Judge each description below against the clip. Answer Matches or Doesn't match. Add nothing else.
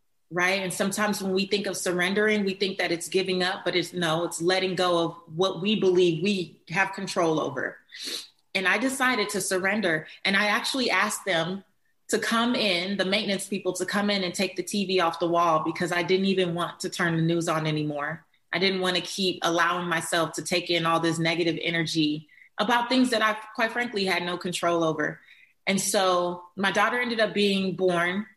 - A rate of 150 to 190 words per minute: Doesn't match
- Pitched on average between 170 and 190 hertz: Matches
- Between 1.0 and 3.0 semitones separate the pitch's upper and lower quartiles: Matches